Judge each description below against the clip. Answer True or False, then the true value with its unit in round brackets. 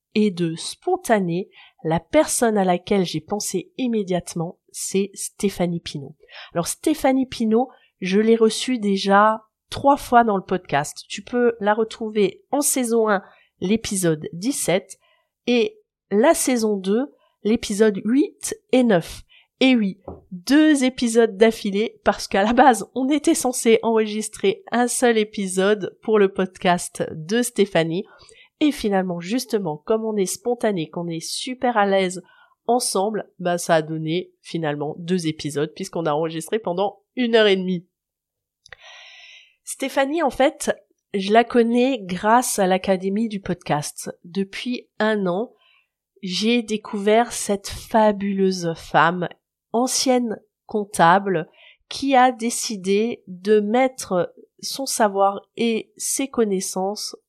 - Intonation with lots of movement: False (4.8 semitones)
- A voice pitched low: False (215 Hz)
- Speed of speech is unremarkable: False (130 wpm)